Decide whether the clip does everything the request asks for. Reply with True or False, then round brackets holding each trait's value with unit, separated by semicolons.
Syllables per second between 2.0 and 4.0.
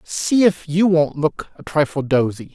False (4.3 syllables/s)